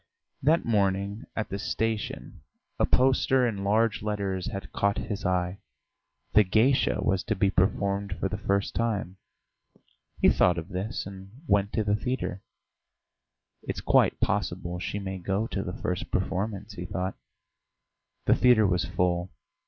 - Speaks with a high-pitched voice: No, low, 100 Hz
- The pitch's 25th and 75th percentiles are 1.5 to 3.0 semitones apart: Yes, narrow, 2.4 semitones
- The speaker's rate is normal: Yes, average, 150 wpm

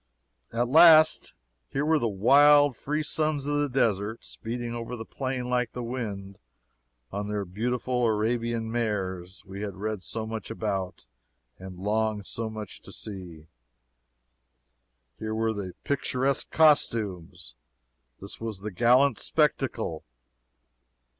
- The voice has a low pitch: Yes, low, 115 Hz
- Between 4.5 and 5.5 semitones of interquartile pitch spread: No, average, 4.0 semitones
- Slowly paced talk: Yes, slow, 125 wpm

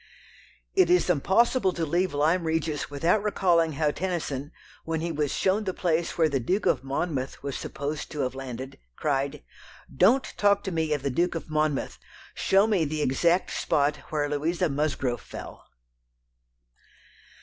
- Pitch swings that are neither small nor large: Yes, average, 4.0 semitones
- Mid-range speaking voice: Yes, medium, 160 Hz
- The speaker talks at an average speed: Yes, average, 160 wpm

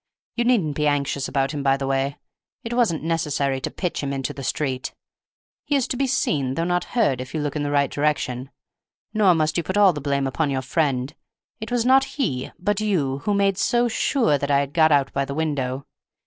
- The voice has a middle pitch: Yes, medium, 150 Hz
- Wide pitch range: Yes, wide, 6.1 semitones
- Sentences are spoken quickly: Yes, fast, 225 wpm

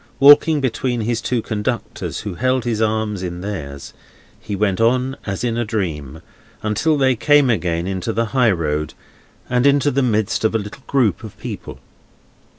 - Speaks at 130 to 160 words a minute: No, average, 170 wpm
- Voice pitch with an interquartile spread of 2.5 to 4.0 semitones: No, average, 4.6 semitones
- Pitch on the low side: Yes, low, 110 Hz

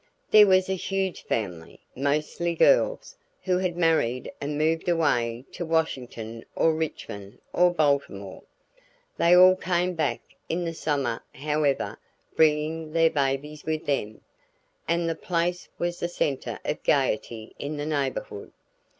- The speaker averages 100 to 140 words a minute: Yes, slow, 135 wpm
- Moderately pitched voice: Yes, medium, 155 Hz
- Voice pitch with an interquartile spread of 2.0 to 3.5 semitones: No, average, 4.0 semitones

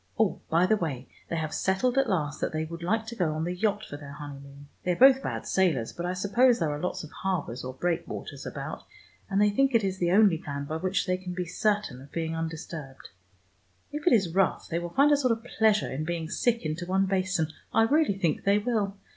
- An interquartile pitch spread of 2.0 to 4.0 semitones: No, average, 4.9 semitones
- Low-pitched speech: No, medium, 180 Hz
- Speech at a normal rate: No, fast, 240 wpm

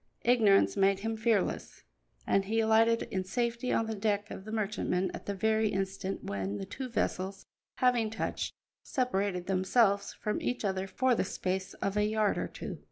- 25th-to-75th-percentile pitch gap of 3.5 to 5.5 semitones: No, average, 2.8 semitones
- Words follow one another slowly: No, average, 175 wpm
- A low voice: No, high, 205 Hz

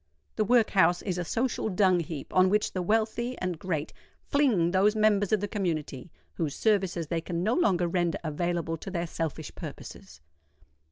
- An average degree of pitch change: Yes, average, 3.8 semitones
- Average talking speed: Yes, average, 170 wpm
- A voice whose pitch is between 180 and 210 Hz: Yes, medium, 185 Hz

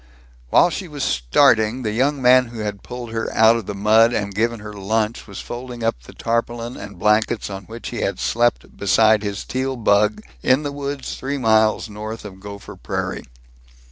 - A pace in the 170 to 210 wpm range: Yes, average, 190 wpm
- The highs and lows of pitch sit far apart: No, average, 2.8 semitones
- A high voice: No, low, 115 Hz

